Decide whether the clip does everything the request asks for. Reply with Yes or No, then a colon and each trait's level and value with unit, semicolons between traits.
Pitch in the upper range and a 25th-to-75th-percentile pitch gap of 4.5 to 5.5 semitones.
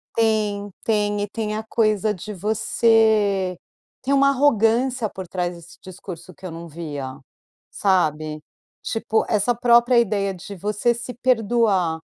No: high, 210 Hz; average, 3.7 semitones